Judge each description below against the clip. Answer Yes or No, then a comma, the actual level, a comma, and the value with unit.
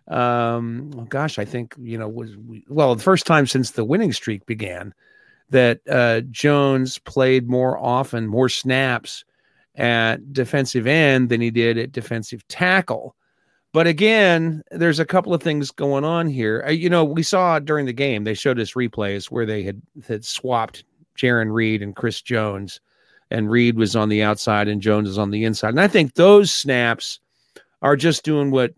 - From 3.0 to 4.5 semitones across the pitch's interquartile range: No, average, 5.0 semitones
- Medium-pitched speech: No, low, 125 Hz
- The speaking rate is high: No, average, 180 wpm